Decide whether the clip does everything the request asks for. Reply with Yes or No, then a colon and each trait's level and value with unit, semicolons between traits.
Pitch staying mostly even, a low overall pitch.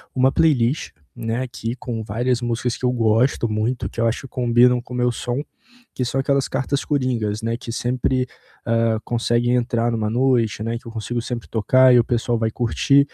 Yes: narrow, 1.7 semitones; low, 120 Hz